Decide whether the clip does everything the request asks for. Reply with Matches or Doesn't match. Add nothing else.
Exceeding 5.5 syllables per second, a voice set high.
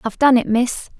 Matches